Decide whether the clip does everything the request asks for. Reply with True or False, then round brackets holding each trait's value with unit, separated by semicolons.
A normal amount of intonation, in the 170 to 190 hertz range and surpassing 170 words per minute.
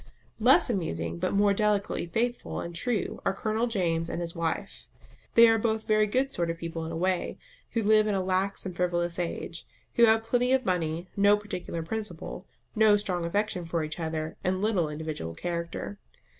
True (4.3 semitones; 185 Hz; 185 wpm)